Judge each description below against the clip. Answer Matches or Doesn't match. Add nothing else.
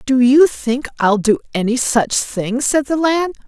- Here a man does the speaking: Doesn't match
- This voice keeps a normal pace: Matches